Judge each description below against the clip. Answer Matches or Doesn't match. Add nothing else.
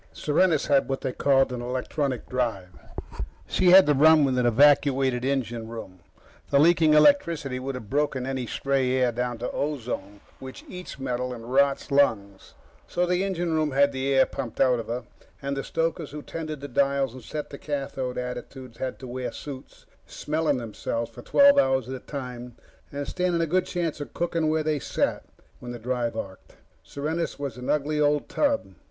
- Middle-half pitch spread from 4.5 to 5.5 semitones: Doesn't match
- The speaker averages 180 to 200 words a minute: Matches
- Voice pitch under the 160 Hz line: Matches